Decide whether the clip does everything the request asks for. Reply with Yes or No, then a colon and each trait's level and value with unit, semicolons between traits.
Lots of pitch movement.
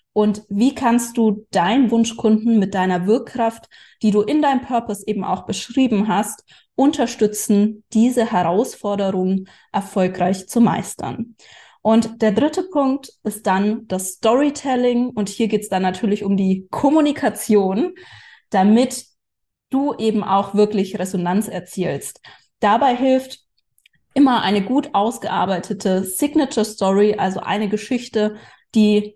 No: average, 3.4 semitones